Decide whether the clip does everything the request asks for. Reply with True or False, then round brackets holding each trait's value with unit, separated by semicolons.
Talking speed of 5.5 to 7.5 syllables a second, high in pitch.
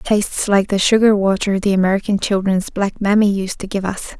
True (5.8 syllables/s; 200 Hz)